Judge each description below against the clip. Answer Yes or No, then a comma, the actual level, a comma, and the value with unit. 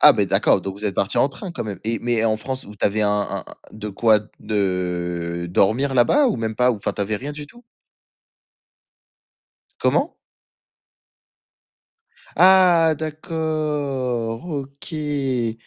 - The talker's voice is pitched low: Yes, low, 120 Hz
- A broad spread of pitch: Yes, wide, 6.1 semitones